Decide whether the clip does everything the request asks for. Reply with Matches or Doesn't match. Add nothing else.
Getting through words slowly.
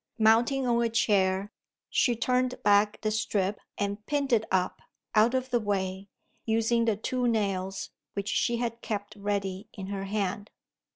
Doesn't match